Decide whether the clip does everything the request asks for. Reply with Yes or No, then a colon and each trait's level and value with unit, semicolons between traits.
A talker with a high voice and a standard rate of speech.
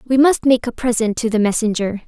No: high, 235 Hz; fast, 230 wpm